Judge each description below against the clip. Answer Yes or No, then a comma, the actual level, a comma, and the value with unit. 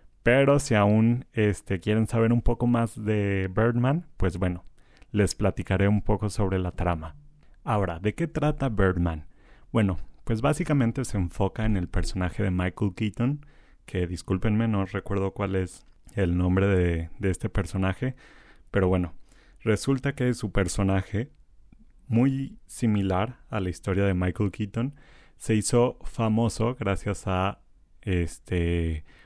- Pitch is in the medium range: No, low, 100 Hz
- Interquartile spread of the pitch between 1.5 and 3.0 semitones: No, average, 3.9 semitones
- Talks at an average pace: Yes, average, 140 wpm